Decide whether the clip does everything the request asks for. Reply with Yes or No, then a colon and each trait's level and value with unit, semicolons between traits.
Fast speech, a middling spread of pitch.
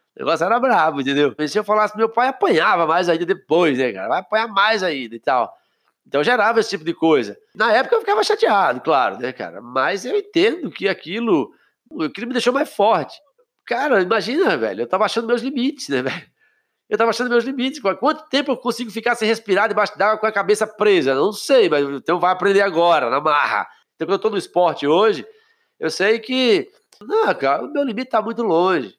No: fast, 215 wpm; wide, 6.6 semitones